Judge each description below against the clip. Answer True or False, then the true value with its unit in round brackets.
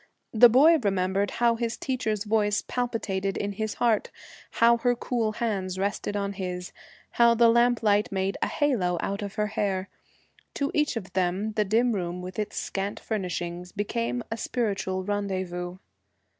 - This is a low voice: False (205 Hz)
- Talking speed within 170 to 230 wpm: False (155 wpm)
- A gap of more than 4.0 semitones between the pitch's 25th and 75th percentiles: False (3.6 semitones)